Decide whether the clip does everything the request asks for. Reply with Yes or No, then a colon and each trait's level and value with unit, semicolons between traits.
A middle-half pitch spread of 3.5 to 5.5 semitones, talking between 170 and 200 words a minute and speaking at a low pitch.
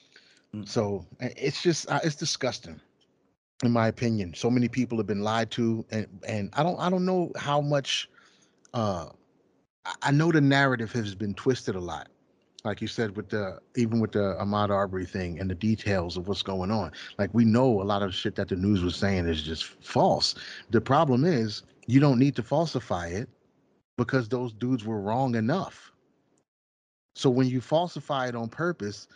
Yes: average, 4.5 semitones; average, 185 wpm; low, 115 Hz